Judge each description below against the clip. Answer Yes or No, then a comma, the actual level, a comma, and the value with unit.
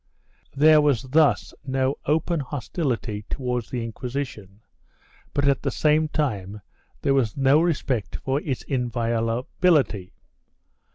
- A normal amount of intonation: Yes, average, 4.2 semitones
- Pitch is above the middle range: No, low, 130 Hz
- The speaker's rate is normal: No, slow, 120 wpm